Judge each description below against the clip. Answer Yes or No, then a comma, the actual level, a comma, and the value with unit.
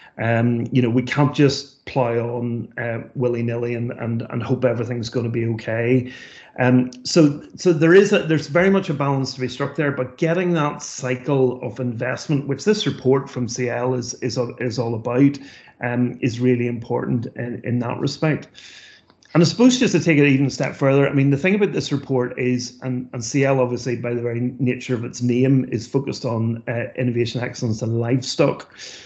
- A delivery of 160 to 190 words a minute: No, average, 200 wpm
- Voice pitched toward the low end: Yes, low, 125 Hz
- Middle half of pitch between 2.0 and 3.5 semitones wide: Yes, narrow, 2.5 semitones